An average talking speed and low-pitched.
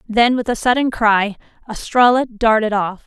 No: average, 155 wpm; high, 225 Hz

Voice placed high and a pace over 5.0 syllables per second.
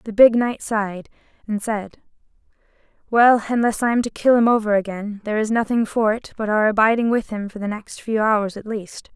Yes: high, 220 Hz; 5.4 syllables/s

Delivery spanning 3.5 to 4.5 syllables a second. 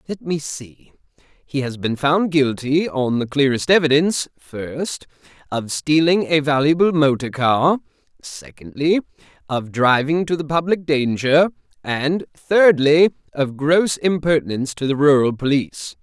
Yes: 4.3 syllables/s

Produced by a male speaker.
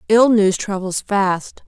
No: female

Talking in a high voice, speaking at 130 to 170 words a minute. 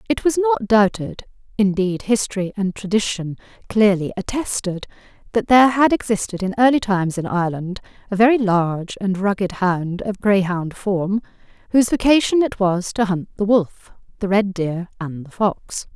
Yes: high, 200 Hz; average, 150 wpm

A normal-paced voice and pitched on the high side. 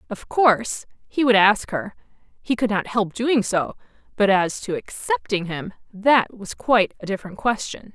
Yes: average, 160 wpm; high, 215 Hz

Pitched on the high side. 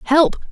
Yes: very high, 285 Hz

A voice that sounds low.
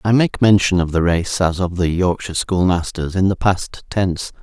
Yes: very low, 90 Hz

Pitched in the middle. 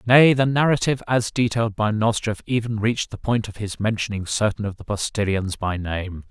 No: low, 110 Hz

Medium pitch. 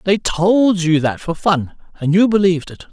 Yes: medium, 175 Hz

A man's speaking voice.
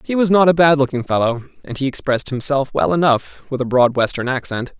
Yes: male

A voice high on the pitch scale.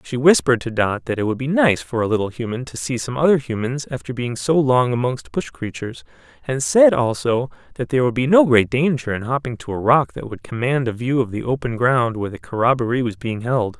No: low, 125 Hz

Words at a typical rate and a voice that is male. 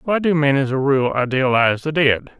No: fast, 225 wpm; male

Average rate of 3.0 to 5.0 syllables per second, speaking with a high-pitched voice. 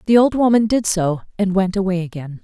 No: 5.6 syllables/s; high, 195 Hz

